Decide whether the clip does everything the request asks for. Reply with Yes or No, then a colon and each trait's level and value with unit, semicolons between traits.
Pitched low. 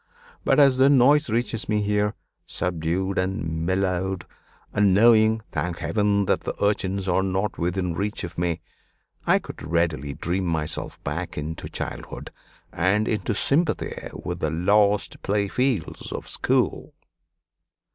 Yes: very low, 95 Hz